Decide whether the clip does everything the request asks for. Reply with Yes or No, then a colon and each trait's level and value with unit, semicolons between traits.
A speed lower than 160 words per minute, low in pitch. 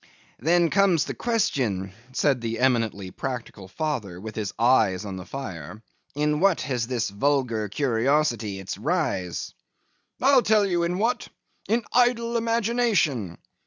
Yes: slow, 135 wpm; low, 130 Hz